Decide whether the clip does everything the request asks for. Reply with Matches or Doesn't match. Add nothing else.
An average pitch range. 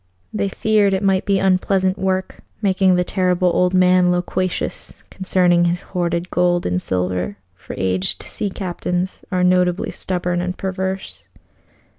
Doesn't match